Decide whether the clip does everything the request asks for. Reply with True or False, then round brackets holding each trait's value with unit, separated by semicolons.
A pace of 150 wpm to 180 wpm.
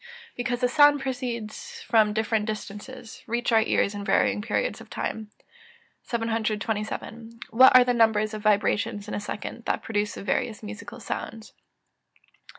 True (155 wpm)